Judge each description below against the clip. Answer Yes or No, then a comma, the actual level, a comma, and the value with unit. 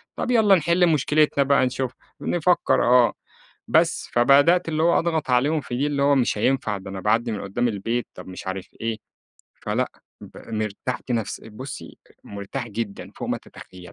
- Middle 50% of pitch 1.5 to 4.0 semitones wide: No, wide, 5.6 semitones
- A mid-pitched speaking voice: No, low, 125 Hz